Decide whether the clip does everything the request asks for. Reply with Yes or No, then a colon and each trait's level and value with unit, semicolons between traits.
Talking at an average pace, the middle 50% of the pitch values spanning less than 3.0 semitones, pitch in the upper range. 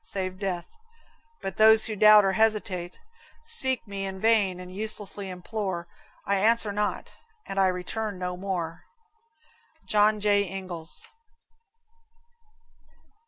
No: slow, 115 wpm; narrow, 2.6 semitones; high, 195 Hz